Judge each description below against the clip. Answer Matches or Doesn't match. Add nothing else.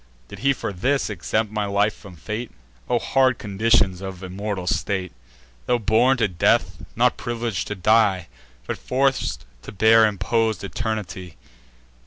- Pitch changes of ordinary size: Matches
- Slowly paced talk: Doesn't match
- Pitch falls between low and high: Doesn't match